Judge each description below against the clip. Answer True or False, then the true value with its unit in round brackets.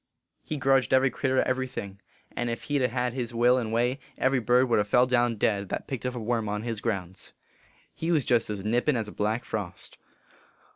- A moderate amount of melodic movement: True (3.0 semitones)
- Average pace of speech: False (225 wpm)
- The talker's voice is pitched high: False (120 Hz)